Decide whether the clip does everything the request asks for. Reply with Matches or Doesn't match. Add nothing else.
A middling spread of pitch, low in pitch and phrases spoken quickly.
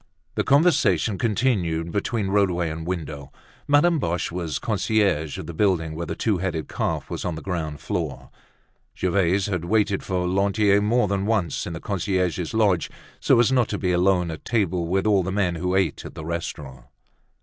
Doesn't match